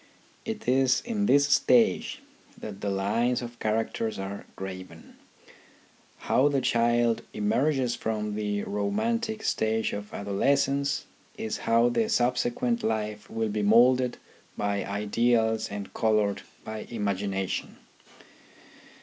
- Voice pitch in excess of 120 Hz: No, low, 110 Hz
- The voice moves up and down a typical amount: Yes, average, 4.0 semitones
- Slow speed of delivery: Yes, slow, 115 wpm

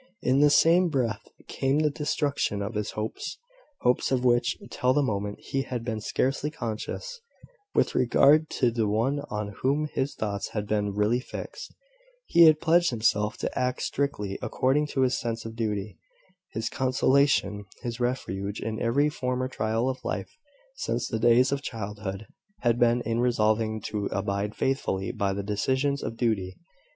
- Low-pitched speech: Yes, low, 120 Hz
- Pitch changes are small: No, average, 4.2 semitones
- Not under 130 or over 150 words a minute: No, average, 165 wpm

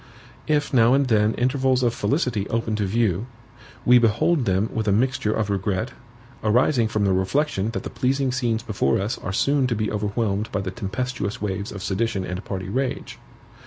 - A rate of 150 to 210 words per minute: Yes, average, 185 wpm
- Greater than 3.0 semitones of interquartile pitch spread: Yes, average, 4.0 semitones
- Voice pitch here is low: Yes, low, 110 Hz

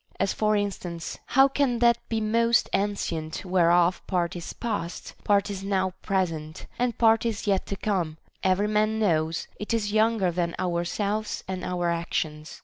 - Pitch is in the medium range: No, high, 195 Hz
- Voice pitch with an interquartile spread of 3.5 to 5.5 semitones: Yes, average, 3.8 semitones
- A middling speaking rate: Yes, average, 165 wpm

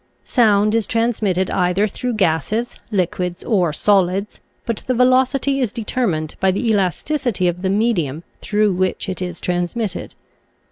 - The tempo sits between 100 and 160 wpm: Yes, average, 145 wpm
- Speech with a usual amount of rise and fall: Yes, average, 4.3 semitones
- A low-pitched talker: No, high, 200 Hz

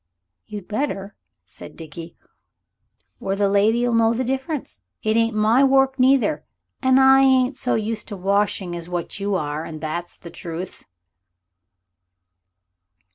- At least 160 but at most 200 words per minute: No, slow, 135 wpm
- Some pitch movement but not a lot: No, wide, 6.2 semitones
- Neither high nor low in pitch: No, high, 215 Hz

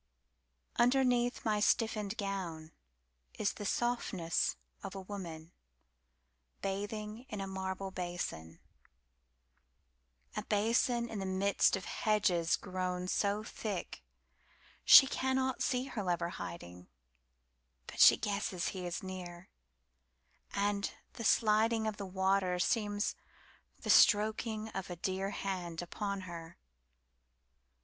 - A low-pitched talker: No, high, 190 Hz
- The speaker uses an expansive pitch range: No, average, 4.8 semitones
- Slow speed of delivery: Yes, slow, 95 wpm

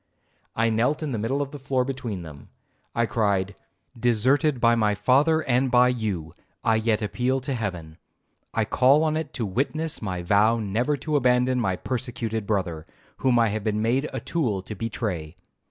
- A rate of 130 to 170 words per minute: No, average, 180 wpm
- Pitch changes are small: No, average, 4.2 semitones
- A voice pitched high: No, low, 115 Hz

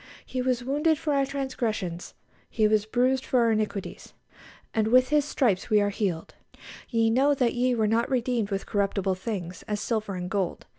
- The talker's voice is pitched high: Yes, high, 225 Hz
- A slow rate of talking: No, average, 185 wpm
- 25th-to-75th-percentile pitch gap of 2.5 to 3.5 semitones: No, average, 4.0 semitones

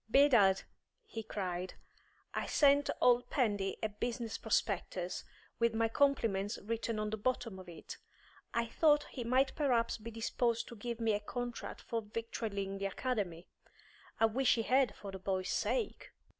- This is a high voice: Yes, high, 225 Hz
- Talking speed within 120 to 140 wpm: No, average, 155 wpm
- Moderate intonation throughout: Yes, average, 3.4 semitones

